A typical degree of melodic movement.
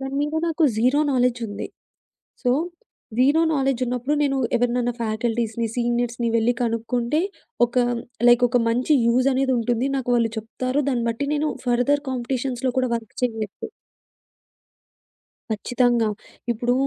No: narrow, 1.9 semitones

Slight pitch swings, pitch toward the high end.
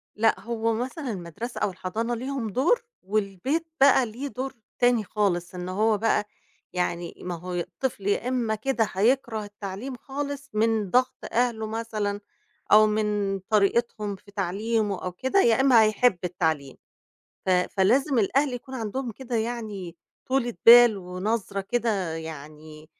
No: average, 4.1 semitones; high, 215 Hz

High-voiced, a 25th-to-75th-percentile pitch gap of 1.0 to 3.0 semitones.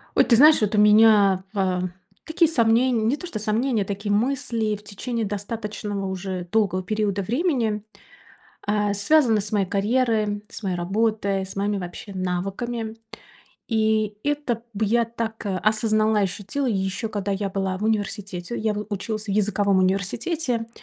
Yes: high, 210 Hz; narrow, 2.4 semitones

